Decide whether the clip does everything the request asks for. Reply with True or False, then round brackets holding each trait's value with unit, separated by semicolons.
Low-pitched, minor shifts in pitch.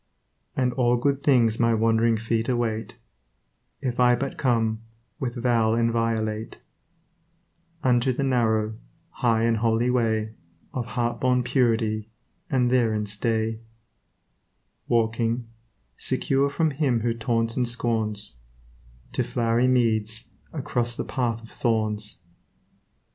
True (115 Hz; 1.9 semitones)